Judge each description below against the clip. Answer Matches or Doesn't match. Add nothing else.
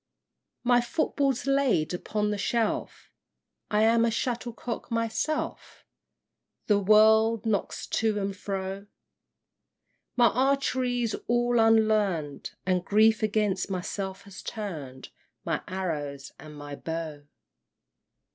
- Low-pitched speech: Doesn't match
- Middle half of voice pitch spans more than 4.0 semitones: Doesn't match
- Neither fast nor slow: Doesn't match